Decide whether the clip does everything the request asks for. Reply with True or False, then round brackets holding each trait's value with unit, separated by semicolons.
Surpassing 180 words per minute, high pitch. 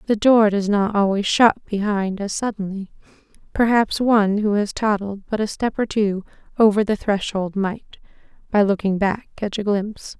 False (170 wpm; 205 Hz)